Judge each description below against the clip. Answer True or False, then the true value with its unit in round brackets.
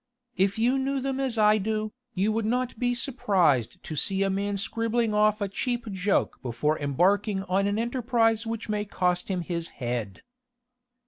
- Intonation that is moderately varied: True (3.6 semitones)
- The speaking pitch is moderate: False (210 Hz)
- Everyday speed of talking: True (175 wpm)